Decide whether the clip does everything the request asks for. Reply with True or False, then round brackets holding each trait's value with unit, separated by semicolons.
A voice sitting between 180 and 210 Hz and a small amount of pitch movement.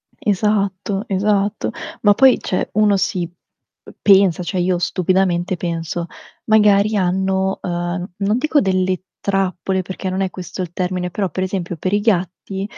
True (190 Hz; 1.9 semitones)